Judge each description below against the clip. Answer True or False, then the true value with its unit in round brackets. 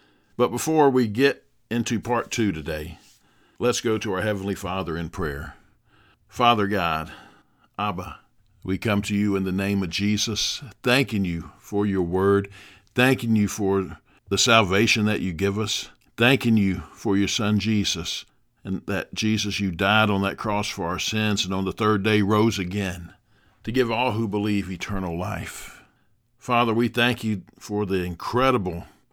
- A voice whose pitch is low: True (105 Hz)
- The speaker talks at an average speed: True (165 wpm)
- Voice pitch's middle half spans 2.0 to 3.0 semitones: True (2.7 semitones)